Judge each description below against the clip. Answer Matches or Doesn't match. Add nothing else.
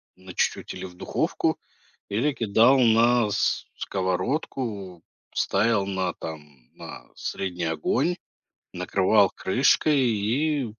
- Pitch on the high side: Doesn't match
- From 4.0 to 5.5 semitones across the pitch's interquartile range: Matches